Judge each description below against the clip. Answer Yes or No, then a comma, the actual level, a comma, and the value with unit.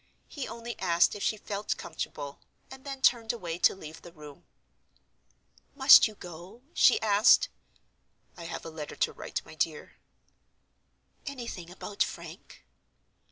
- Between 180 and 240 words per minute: No, average, 140 wpm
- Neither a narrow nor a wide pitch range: No, wide, 5.8 semitones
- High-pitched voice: Yes, high, 200 Hz